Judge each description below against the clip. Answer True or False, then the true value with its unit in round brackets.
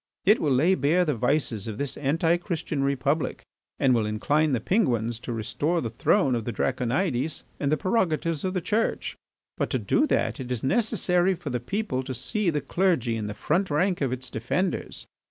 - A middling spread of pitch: False (6.3 semitones)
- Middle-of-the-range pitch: True (145 Hz)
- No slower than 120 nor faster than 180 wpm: False (195 wpm)